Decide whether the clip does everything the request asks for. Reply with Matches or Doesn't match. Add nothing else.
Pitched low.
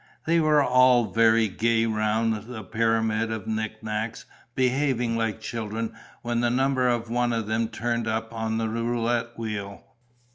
Matches